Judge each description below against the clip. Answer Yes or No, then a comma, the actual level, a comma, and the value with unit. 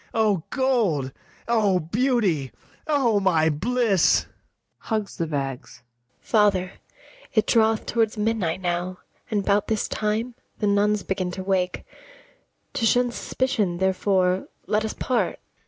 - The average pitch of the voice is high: Yes, high, 205 Hz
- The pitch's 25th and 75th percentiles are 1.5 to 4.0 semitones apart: Yes, average, 3.6 semitones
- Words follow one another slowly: Yes, slow, 125 wpm